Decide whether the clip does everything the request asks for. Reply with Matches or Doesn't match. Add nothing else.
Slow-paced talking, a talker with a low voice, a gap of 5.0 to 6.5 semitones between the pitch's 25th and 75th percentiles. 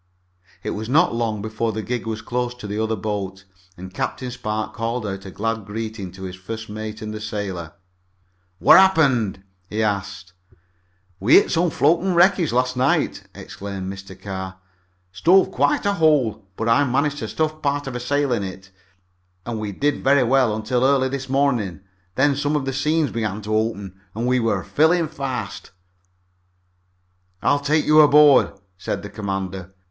Doesn't match